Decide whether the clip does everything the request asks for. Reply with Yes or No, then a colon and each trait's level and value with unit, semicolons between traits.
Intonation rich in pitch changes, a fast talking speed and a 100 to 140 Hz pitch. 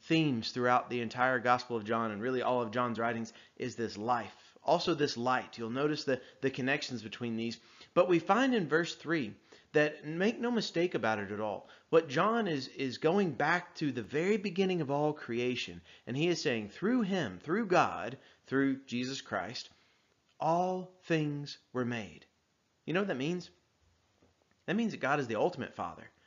No: wide, 6.2 semitones; average, 185 wpm; low, 135 Hz